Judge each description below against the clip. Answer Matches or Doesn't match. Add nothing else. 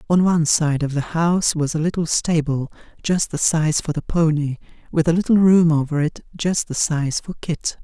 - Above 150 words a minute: Matches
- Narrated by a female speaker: Doesn't match